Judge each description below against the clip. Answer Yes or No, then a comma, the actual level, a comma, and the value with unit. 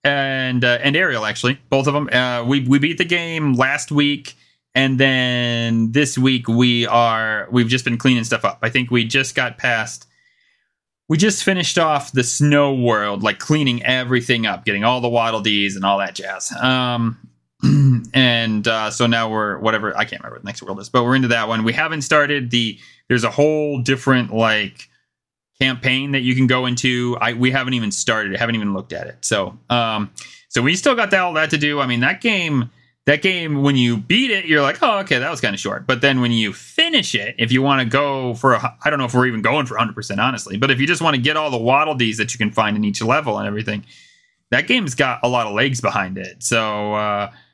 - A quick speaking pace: Yes, fast, 230 wpm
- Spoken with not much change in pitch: No, average, 3.6 semitones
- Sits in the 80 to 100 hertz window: No, low, 125 Hz